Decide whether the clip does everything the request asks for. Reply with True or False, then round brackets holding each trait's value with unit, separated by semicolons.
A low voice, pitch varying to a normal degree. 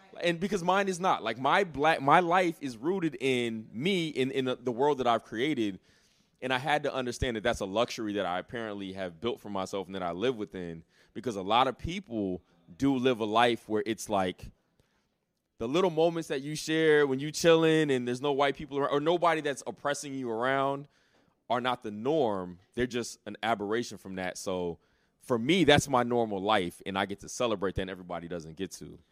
False (120 Hz; 6.2 semitones)